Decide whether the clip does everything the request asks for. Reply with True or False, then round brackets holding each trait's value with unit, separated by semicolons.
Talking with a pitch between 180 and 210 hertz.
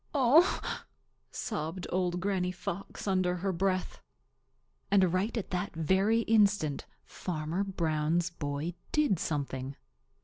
True (185 Hz)